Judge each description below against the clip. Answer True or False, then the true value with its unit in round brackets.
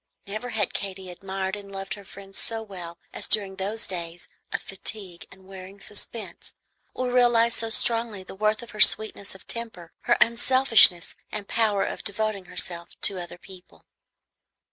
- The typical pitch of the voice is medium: False (200 Hz)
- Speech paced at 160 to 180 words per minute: True (165 wpm)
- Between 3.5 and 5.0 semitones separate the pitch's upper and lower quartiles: False (2.9 semitones)